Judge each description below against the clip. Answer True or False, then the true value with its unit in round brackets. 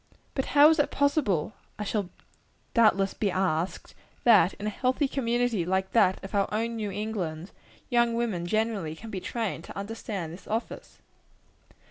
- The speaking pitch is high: True (210 Hz)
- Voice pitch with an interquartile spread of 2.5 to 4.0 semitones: True (3.6 semitones)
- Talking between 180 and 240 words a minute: False (160 wpm)